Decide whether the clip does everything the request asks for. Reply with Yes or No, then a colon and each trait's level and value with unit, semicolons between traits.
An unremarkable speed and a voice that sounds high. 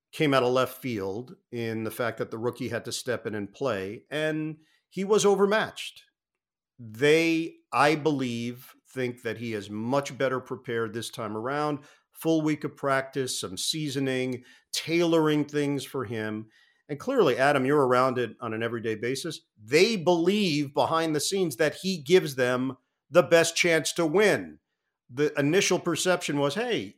No: average, 160 wpm; medium, 140 Hz